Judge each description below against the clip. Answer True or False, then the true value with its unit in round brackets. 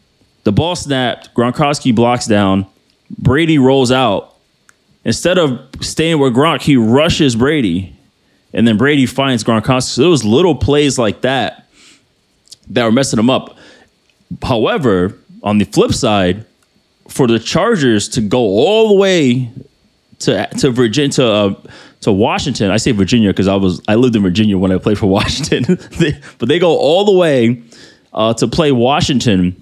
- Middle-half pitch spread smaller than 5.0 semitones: False (5.3 semitones)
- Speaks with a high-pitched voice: False (120 Hz)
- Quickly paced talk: False (160 wpm)